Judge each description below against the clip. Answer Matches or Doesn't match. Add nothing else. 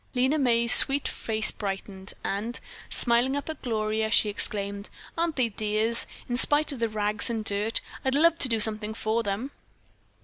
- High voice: Matches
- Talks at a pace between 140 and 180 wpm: Matches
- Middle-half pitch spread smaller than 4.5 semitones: Matches